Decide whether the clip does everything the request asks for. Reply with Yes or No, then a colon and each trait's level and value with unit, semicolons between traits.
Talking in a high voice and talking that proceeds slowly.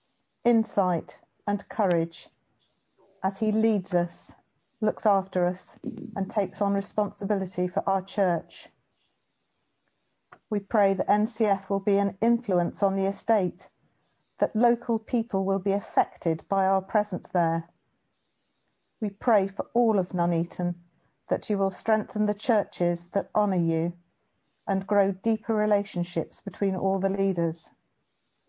Yes: high, 195 Hz; slow, 130 wpm